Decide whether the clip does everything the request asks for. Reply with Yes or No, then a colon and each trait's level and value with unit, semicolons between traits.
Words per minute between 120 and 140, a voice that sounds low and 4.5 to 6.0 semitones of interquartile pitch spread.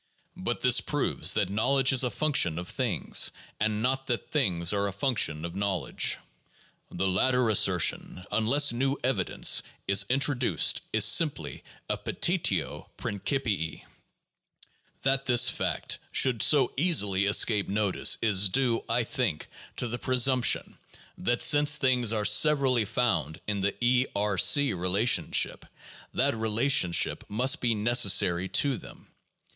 Yes: slow, 135 wpm; low, 115 Hz; average, 4.9 semitones